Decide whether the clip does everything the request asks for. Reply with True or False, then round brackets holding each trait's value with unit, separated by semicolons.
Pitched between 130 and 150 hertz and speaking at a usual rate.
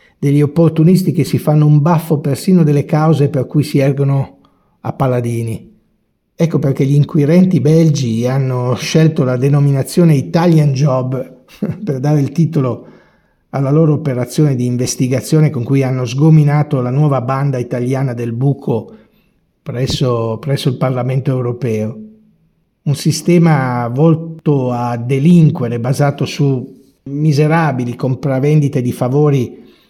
True (140 Hz; 125 wpm)